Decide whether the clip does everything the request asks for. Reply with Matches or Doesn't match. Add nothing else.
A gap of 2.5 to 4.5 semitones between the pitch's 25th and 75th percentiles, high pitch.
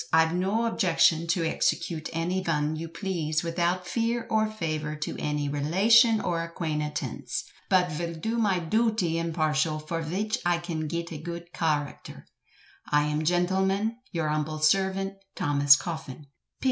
Doesn't match